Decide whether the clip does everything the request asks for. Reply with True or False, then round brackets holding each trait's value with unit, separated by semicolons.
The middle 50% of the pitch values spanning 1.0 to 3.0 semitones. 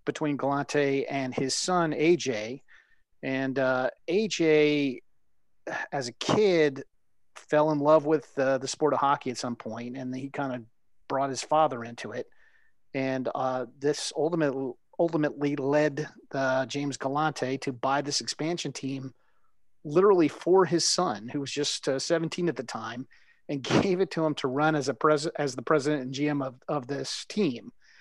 True (2.7 semitones)